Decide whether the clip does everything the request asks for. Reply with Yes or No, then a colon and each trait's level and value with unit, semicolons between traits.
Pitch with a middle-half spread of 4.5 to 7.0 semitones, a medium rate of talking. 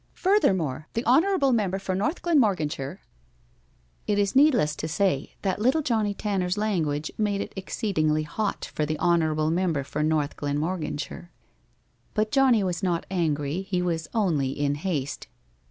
Yes: wide, 5.5 semitones; average, 145 wpm